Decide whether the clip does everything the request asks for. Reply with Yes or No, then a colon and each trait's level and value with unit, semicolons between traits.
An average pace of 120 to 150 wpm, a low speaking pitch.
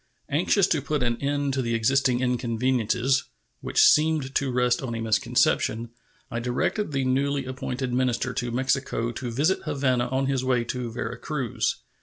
No: average, 165 wpm; low, 130 Hz